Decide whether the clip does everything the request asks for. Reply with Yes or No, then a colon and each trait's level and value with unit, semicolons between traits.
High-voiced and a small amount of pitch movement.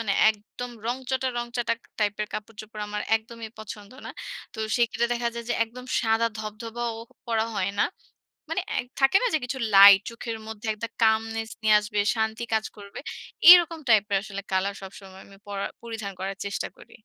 Yes: high, 220 Hz; narrow, 2.3 semitones